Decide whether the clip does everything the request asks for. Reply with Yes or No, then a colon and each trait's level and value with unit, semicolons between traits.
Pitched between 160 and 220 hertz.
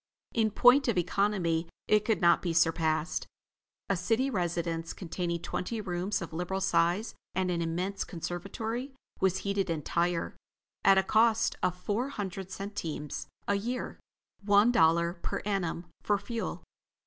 Yes: high, 190 Hz